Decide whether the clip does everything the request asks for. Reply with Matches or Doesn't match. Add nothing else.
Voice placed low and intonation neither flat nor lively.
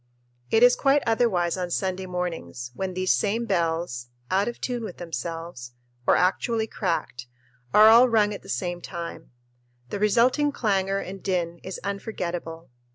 Doesn't match